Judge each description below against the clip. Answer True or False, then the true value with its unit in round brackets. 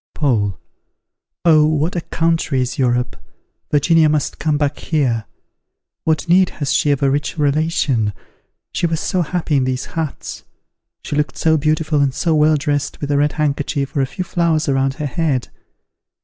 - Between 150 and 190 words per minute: True (170 wpm)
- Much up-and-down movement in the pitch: False (2.7 semitones)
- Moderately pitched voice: True (150 Hz)